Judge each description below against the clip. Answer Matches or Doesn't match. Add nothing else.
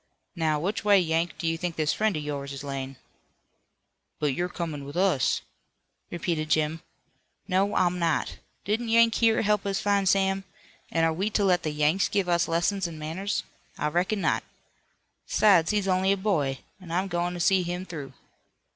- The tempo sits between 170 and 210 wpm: Matches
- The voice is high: Doesn't match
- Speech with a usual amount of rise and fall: Matches